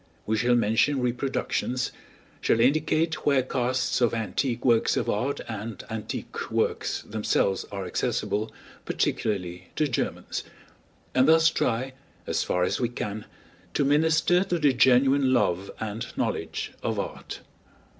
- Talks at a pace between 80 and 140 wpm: Yes, slow, 135 wpm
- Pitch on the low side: Yes, low, 125 Hz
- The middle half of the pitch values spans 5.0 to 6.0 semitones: No, average, 4.3 semitones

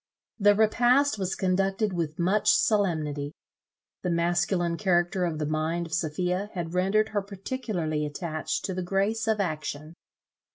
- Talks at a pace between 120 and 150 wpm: Yes, average, 140 wpm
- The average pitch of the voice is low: No, medium, 180 Hz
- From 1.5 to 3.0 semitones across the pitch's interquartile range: No, average, 3.7 semitones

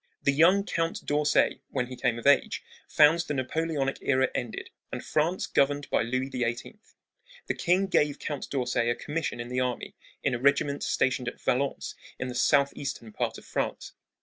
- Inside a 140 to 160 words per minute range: No, average, 175 wpm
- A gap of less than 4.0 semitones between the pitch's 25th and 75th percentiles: Yes, average, 3.0 semitones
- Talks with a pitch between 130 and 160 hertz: Yes, medium, 140 Hz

